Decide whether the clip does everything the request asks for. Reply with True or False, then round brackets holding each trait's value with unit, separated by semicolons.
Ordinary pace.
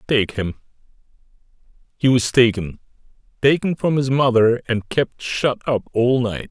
False (130 wpm)